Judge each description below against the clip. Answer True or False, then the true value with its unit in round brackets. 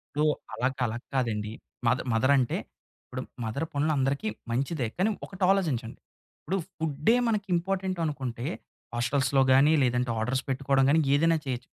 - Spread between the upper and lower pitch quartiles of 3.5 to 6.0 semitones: True (4.5 semitones)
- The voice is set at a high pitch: False (135 Hz)